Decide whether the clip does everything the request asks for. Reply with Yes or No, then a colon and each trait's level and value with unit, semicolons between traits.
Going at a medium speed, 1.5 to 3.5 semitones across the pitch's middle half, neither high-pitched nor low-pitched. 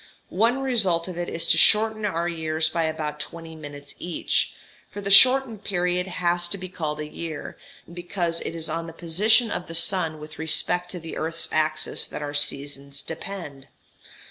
Yes: average, 180 wpm; average, 2.9 semitones; medium, 165 Hz